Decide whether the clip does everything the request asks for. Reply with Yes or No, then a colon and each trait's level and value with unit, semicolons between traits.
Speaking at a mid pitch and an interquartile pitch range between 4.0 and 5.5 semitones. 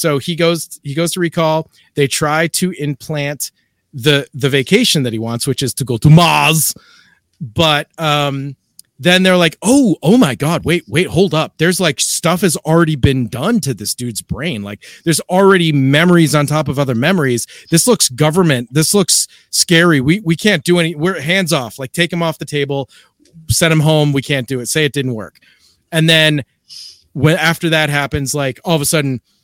No: medium, 155 Hz; average, 3.4 semitones